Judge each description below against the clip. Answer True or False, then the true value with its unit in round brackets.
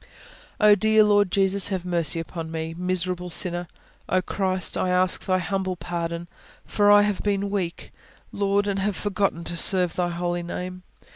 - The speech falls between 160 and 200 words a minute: True (165 wpm)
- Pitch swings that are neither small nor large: False (2.3 semitones)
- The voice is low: False (185 Hz)